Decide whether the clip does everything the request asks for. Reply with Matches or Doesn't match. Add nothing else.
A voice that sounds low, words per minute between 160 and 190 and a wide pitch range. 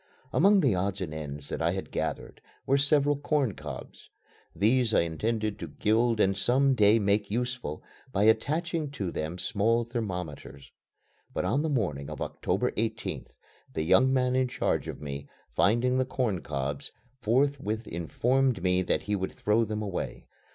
Matches